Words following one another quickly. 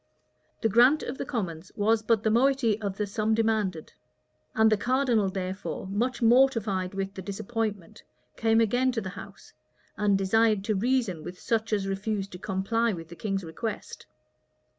No: average, 165 wpm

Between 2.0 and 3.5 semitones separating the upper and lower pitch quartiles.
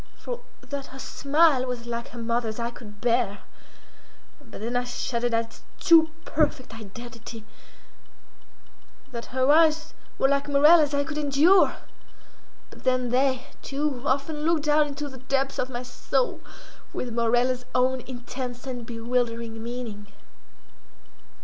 Yes: average, 3.1 semitones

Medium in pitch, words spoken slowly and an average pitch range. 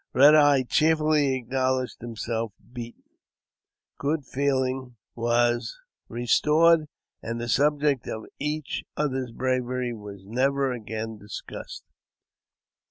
No: low, 130 Hz; slow, 100 wpm; average, 3.4 semitones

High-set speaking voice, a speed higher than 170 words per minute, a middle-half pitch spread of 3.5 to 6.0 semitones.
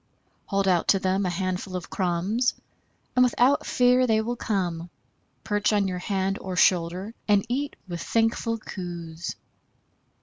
No: high, 195 Hz; average, 145 wpm; average, 3.9 semitones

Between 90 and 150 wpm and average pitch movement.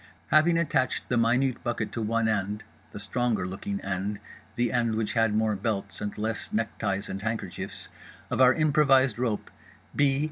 No: average, 165 wpm; average, 3.3 semitones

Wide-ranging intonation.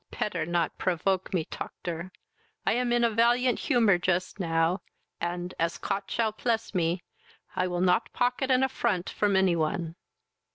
No: average, 4.9 semitones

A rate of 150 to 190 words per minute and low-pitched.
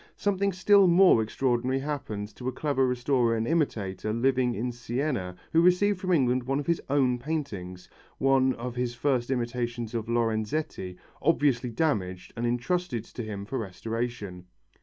Yes: average, 155 wpm; low, 125 Hz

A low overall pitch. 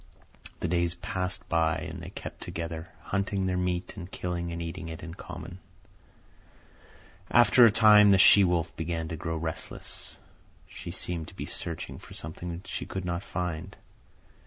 Yes: very low, 85 Hz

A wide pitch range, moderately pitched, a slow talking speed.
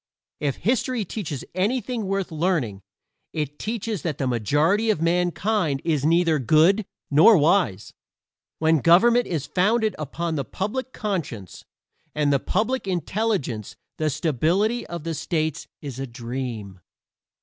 Yes: wide, 6.4 semitones; medium, 165 Hz; slow, 125 wpm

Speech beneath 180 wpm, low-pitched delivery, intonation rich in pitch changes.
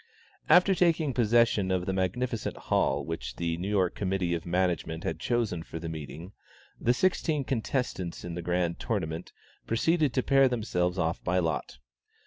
Yes: average, 160 wpm; very low, 95 Hz; wide, 6.3 semitones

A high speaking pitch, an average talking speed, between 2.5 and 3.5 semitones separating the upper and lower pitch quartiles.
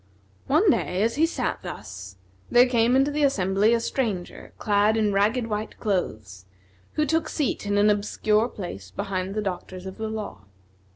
No: high, 210 Hz; average, 170 wpm; average, 4.2 semitones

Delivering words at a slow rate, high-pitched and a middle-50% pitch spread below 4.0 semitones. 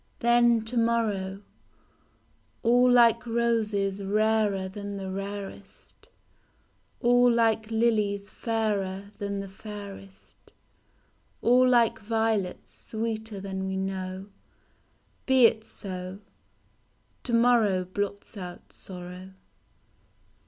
Yes: slow, 95 wpm; high, 210 Hz; average, 3.0 semitones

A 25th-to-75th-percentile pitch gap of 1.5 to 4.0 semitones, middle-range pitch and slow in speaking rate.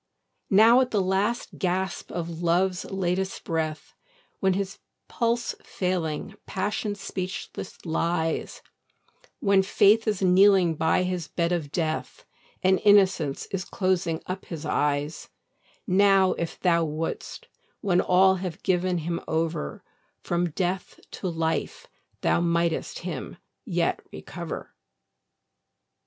Yes: narrow, 2.6 semitones; medium, 180 Hz; slow, 115 wpm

